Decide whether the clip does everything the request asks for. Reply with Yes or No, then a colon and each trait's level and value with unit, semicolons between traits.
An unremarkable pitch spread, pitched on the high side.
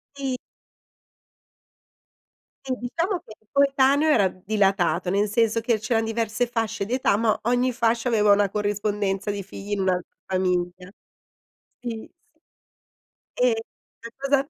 Yes: average, 3.6 semitones; high, 220 Hz